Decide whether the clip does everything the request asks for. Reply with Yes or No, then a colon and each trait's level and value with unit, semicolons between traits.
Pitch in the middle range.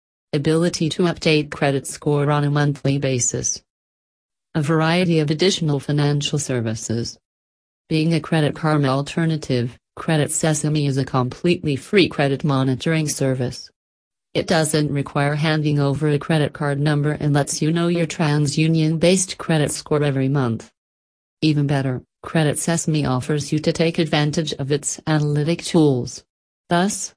Yes: medium, 150 Hz